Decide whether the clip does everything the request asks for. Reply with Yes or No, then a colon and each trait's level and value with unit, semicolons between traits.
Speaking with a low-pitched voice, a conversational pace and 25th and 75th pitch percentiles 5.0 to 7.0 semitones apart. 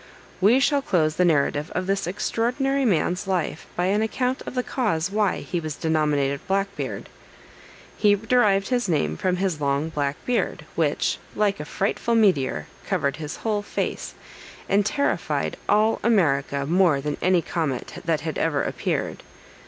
No: medium, 185 Hz; average, 160 wpm; wide, 5.6 semitones